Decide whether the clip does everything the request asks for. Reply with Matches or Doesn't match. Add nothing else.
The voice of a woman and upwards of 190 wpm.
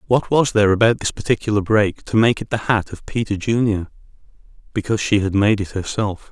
Doesn't match